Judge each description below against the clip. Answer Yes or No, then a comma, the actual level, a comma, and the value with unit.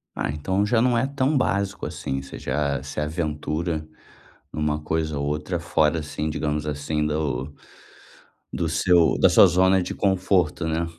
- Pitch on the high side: No, very low, 80 Hz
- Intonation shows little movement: No, average, 3.5 semitones